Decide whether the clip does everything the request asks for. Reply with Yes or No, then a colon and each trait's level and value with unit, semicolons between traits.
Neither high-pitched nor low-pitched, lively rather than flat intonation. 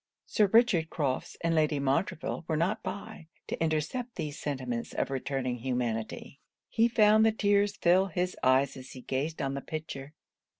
Yes: medium, 155 Hz; wide, 6.4 semitones